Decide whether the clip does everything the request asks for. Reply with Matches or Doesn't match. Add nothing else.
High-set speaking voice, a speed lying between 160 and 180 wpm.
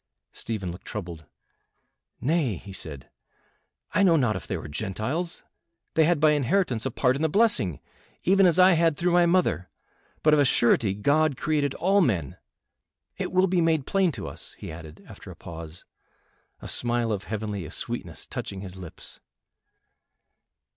Doesn't match